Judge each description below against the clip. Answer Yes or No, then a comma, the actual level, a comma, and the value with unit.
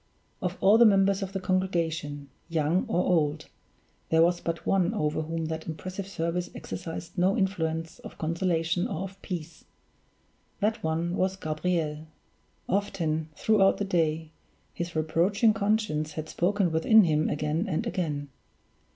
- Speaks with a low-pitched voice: No, medium, 170 Hz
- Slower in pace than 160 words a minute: Yes, average, 140 wpm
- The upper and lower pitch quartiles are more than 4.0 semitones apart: No, average, 3.3 semitones